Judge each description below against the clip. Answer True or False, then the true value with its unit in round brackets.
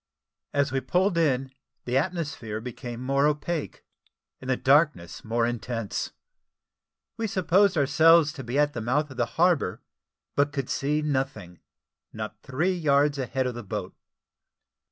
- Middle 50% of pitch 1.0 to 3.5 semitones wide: False (4.0 semitones)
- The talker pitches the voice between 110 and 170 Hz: True (140 Hz)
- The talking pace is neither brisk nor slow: True (150 wpm)